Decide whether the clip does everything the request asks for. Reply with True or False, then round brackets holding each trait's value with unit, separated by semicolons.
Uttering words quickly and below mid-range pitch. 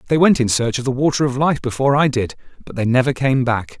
True (270 wpm; 130 Hz)